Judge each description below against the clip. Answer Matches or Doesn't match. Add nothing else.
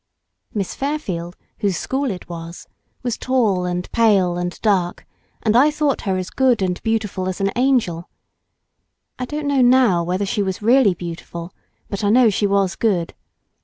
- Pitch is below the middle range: Doesn't match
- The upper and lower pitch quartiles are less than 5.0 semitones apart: Doesn't match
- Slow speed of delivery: Doesn't match